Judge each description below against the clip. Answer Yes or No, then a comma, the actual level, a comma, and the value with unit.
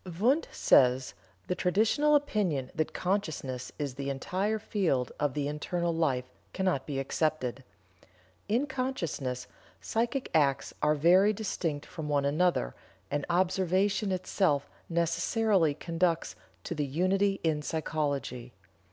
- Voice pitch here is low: No, medium, 165 Hz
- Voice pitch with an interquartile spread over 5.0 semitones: Yes, wide, 5.5 semitones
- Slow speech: Yes, slow, 115 wpm